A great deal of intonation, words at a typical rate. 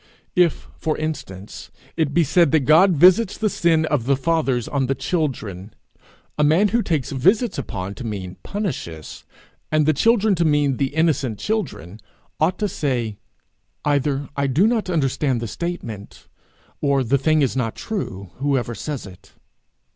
Yes: wide, 5.7 semitones; average, 160 wpm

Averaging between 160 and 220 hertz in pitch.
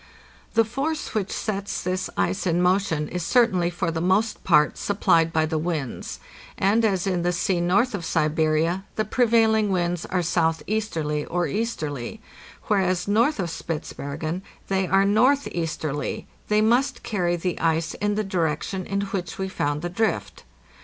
Yes: medium, 185 Hz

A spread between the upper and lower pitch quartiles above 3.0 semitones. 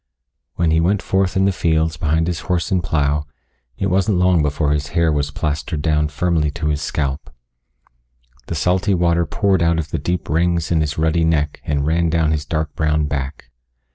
No: narrow, 2.4 semitones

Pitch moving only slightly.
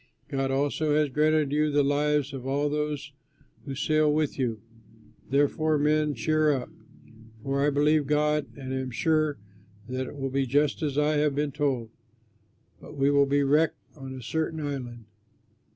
Yes: narrow, 1.9 semitones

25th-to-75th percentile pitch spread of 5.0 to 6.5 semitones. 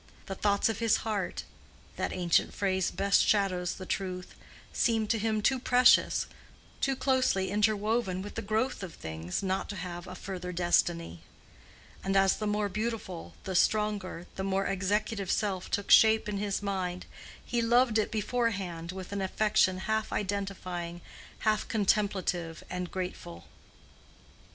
No: average, 2.8 semitones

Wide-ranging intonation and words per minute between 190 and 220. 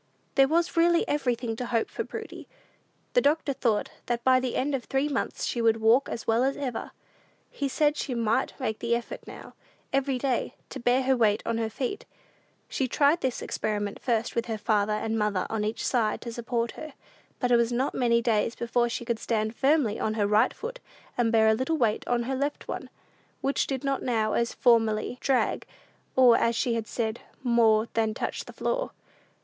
No: average, 3.0 semitones; average, 200 wpm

